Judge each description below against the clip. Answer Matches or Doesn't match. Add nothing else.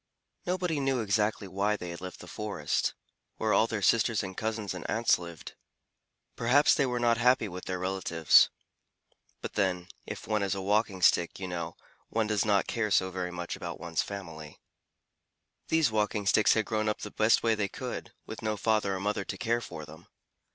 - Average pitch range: Matches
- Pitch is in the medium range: Doesn't match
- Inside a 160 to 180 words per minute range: Doesn't match